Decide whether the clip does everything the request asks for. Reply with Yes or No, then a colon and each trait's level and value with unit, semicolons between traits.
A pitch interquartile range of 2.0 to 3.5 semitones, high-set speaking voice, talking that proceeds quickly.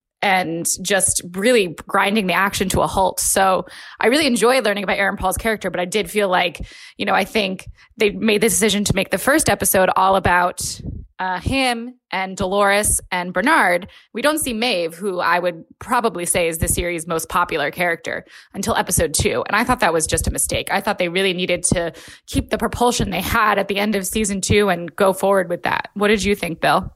Yes: average, 2.9 semitones; high, 195 Hz; fast, 215 wpm